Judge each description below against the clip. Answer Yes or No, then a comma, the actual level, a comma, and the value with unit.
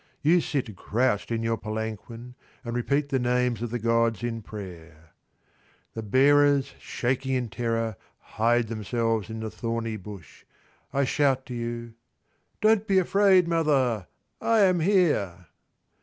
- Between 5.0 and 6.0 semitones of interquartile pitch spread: No, average, 4.0 semitones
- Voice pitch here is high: No, low, 120 Hz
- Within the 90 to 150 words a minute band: Yes, average, 140 wpm